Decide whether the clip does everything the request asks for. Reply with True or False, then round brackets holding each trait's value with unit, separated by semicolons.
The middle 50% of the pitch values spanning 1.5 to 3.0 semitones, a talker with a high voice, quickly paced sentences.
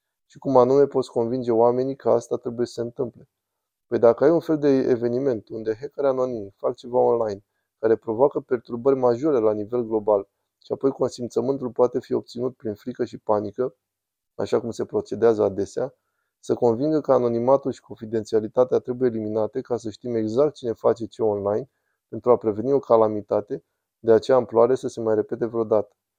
False (2.7 semitones; 120 Hz; 175 wpm)